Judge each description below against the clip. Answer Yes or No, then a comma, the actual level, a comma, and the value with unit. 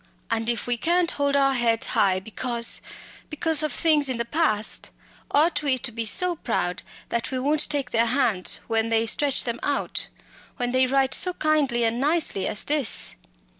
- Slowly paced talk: No, average, 180 wpm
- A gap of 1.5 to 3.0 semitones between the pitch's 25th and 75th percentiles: No, average, 4.3 semitones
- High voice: Yes, very high, 255 Hz